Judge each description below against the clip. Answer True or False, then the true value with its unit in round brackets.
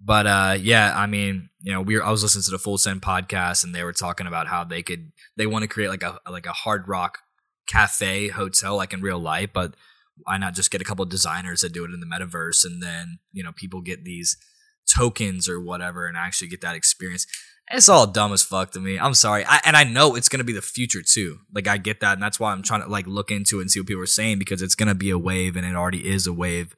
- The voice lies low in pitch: True (95 Hz)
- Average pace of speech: False (275 wpm)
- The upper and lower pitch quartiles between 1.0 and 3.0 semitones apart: True (2.6 semitones)